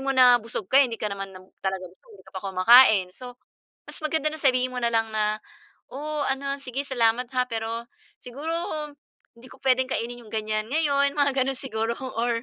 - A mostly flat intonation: No, average, 3.5 semitones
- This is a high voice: Yes, high, 245 Hz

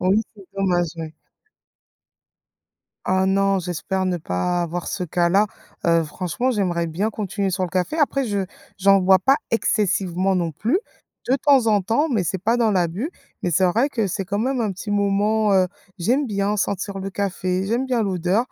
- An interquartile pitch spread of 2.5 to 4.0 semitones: Yes, average, 3.2 semitones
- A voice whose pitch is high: Yes, high, 195 Hz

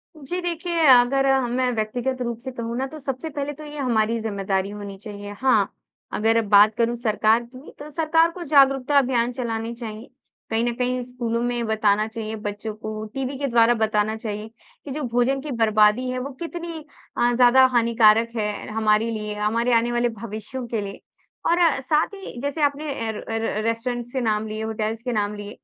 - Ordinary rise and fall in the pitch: Yes, average, 3.3 semitones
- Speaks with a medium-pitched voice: No, high, 235 Hz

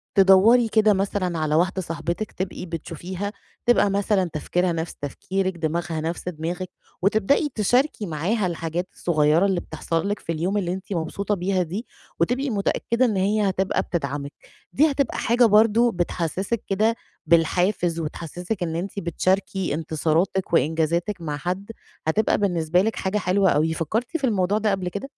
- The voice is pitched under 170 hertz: No, medium, 185 Hz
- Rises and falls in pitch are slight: No, average, 3.7 semitones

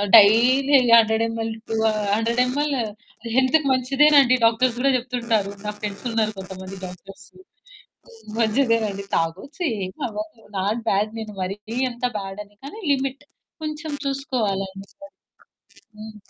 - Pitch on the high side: Yes, high, 225 Hz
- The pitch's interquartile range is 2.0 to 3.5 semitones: No, average, 4.3 semitones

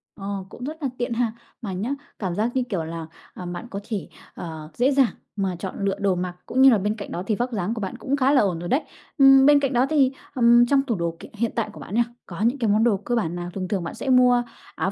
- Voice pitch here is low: No, high, 220 Hz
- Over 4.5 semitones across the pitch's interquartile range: Yes, average, 5.1 semitones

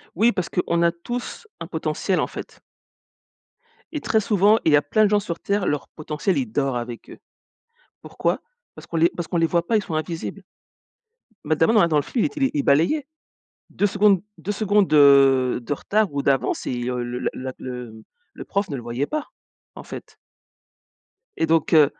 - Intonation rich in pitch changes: Yes, wide, 6.6 semitones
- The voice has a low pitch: No, medium, 165 Hz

